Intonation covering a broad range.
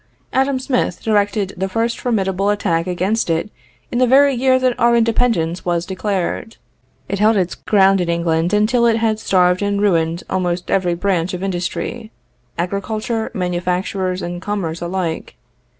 No: average, 4.0 semitones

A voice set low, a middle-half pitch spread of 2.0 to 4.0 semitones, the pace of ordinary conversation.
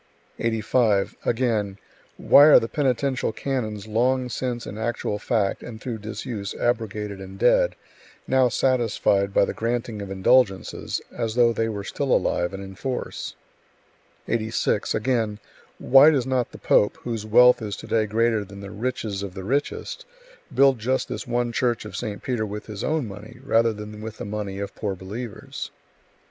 Yes: low, 110 Hz; average, 3.1 semitones; average, 165 wpm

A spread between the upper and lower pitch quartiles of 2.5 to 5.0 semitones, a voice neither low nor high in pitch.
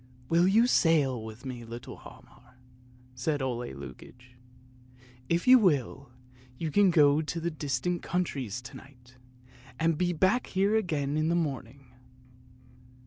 No: wide, 5.5 semitones; medium, 145 Hz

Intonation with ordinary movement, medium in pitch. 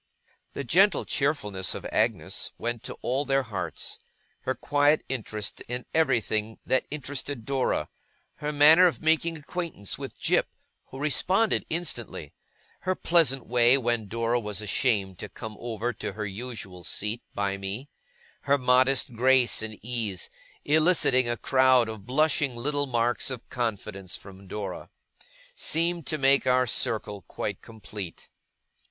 No: average, 4.9 semitones; low, 125 Hz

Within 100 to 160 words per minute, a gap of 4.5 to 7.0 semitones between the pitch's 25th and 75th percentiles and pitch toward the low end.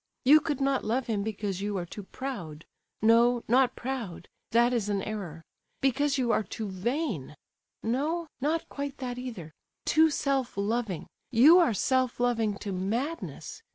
No: average, 150 wpm; average, 5.0 semitones; high, 240 Hz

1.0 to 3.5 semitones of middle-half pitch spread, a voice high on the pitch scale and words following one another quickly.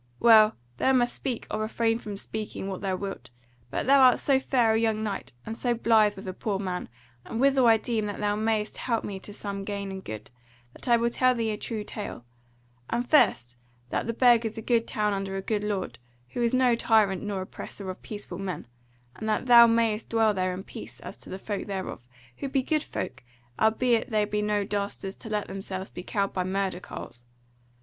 Yes: average, 3.0 semitones; high, 215 Hz; fast, 215 wpm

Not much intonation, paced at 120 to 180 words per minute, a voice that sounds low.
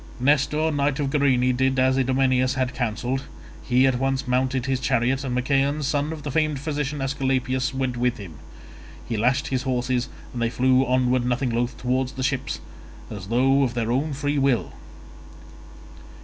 Yes: narrow, 1.7 semitones; average, 170 wpm; low, 130 Hz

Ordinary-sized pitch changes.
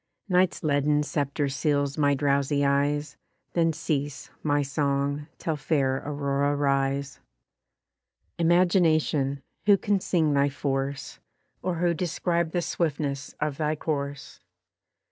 No: narrow, 2.2 semitones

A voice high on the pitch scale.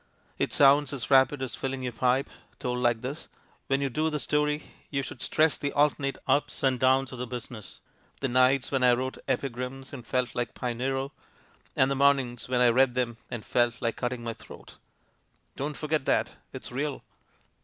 No: low, 130 Hz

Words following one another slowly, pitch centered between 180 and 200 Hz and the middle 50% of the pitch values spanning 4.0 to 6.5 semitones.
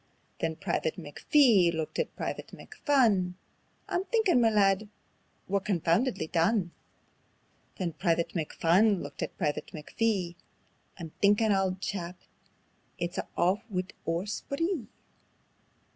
Yes: slow, 115 wpm; high, 190 Hz; average, 4.5 semitones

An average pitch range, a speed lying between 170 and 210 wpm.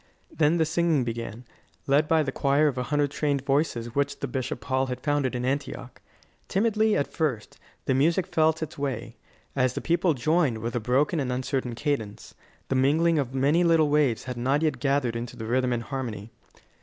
Yes: average, 3.6 semitones; average, 185 wpm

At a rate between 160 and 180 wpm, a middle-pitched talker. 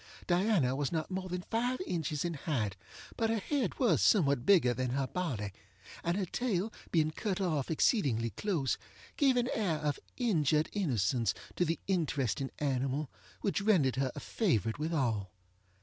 Yes: average, 165 wpm; medium, 160 Hz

